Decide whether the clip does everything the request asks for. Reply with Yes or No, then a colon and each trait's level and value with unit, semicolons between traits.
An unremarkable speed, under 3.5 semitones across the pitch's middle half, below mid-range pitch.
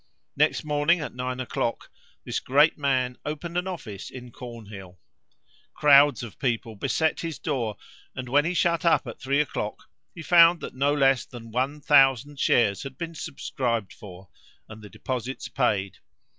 No: average, 160 wpm; average, 4.1 semitones; low, 130 Hz